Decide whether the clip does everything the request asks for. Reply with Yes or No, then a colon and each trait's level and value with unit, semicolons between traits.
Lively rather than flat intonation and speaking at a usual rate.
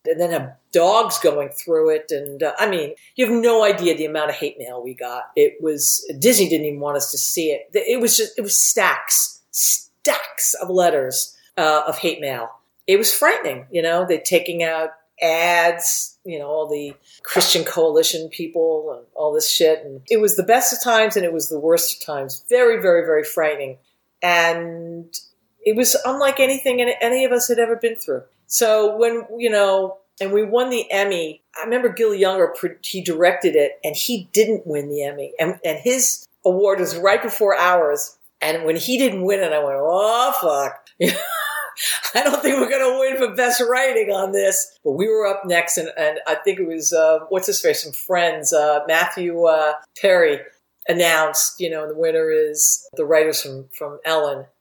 Yes: wide, 8.1 semitones; average, 195 wpm